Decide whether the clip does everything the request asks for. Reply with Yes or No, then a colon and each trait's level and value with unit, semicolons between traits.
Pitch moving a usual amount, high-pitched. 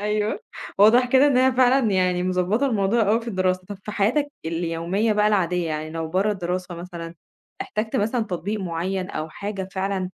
Yes: average, 3.3 semitones; high, 195 Hz